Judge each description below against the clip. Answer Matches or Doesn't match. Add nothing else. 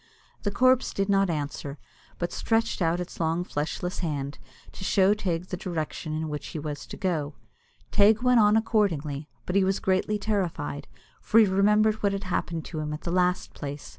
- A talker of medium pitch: Matches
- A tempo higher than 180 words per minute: Matches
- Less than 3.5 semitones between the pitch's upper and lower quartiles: Doesn't match